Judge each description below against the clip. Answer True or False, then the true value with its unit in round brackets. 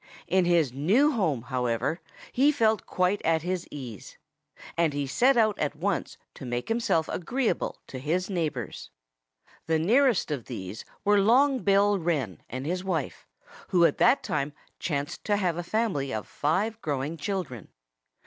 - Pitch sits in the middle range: True (170 Hz)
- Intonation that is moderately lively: False (6.5 semitones)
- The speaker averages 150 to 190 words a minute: True (160 wpm)